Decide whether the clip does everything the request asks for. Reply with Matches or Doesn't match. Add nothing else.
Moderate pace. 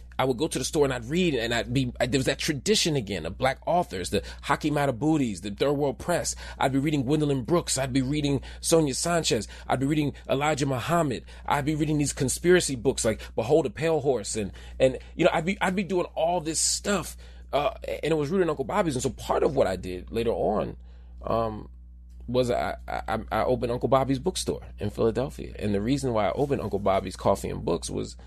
Doesn't match